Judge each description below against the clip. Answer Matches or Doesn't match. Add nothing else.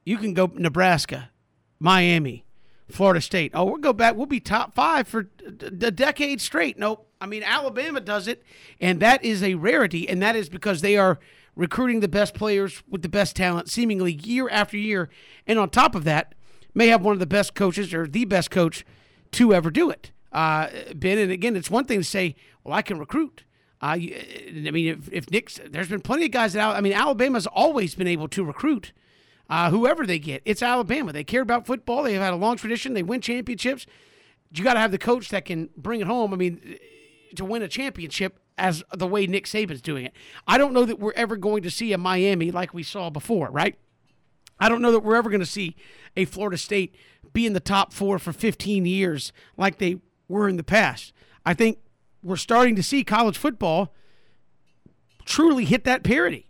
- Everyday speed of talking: Doesn't match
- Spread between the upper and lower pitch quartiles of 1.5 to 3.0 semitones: Doesn't match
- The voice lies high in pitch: Matches